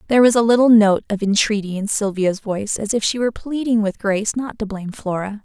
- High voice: Yes, high, 215 Hz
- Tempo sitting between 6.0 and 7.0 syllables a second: Yes, 6.2 syllables/s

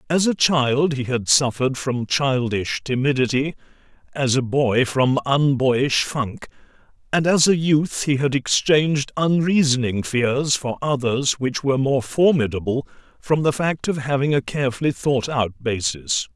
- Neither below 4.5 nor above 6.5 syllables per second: No, 4.3 syllables/s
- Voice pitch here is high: No, low, 135 Hz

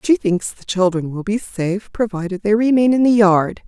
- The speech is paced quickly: Yes, fast, 215 wpm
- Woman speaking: Yes, female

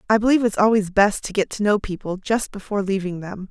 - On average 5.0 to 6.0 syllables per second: No, 6.3 syllables/s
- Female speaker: Yes, female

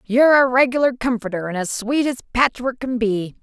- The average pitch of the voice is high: Yes, high, 240 Hz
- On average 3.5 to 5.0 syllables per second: No, 5.5 syllables/s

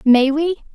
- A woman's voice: Yes, female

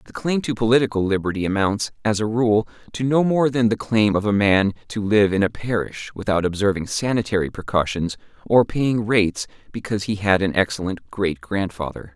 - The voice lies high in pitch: No, low, 105 Hz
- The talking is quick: No, average, 185 wpm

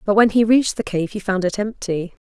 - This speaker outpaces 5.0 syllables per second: Yes, 5.8 syllables/s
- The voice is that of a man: No, female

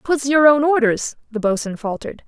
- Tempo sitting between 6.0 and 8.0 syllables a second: No, 5.4 syllables/s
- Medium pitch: No, very high, 255 Hz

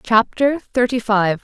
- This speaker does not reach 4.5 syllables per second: Yes, 3.8 syllables/s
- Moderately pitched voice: No, high, 230 Hz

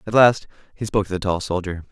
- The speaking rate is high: Yes, fast, 250 wpm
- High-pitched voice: No, very low, 95 Hz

